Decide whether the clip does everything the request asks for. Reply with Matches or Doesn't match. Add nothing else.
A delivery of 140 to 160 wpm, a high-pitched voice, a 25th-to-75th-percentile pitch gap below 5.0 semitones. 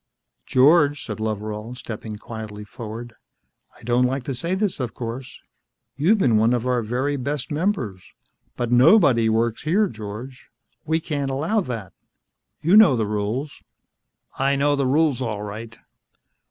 Doesn't match